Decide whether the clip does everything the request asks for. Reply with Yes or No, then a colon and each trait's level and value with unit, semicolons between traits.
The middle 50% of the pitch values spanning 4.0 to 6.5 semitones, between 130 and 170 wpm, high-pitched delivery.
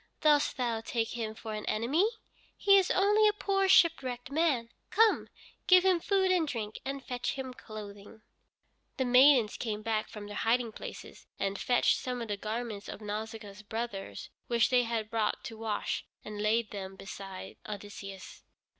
Yes: average, 4.6 semitones; average, 165 wpm; high, 230 Hz